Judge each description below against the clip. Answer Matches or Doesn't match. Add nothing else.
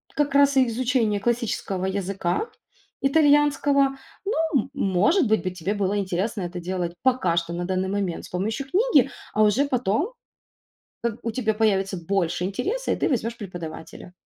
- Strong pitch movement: Matches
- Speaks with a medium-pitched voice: Doesn't match